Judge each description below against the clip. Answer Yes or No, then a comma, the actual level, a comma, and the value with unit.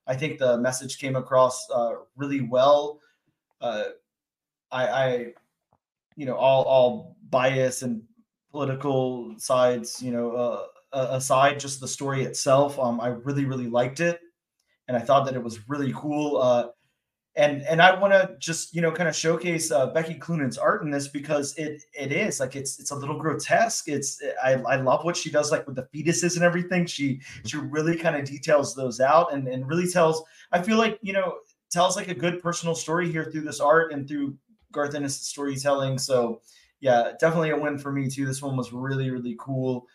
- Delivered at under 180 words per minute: No, average, 195 wpm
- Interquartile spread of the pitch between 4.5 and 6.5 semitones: No, average, 4.0 semitones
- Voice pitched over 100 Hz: Yes, medium, 140 Hz